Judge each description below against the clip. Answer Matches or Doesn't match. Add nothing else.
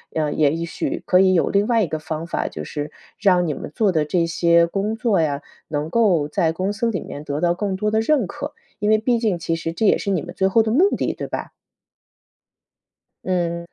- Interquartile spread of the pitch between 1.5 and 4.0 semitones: Doesn't match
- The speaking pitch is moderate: Matches